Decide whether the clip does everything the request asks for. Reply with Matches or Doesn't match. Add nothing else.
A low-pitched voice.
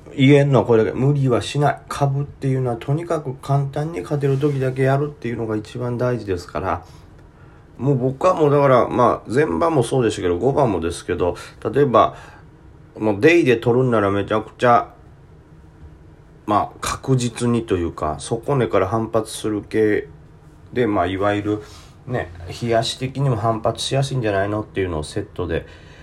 Matches